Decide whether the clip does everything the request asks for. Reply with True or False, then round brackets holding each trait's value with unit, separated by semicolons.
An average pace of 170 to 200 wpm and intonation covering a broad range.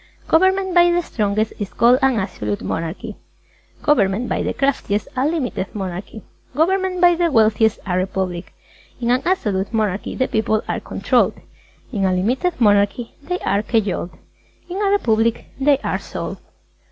False (155 wpm; 7.6 semitones)